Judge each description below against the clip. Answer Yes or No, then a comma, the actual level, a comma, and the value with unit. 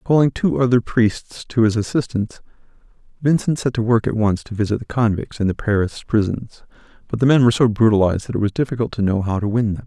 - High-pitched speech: No, low, 115 Hz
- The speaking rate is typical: No, fast, 225 wpm